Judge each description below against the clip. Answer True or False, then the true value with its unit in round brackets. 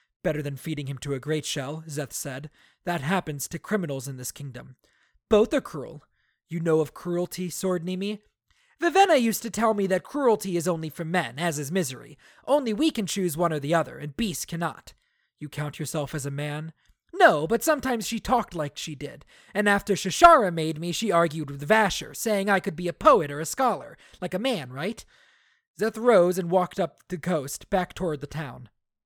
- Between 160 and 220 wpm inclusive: True (200 wpm)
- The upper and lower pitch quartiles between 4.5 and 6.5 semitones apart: True (5.6 semitones)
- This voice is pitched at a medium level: True (175 Hz)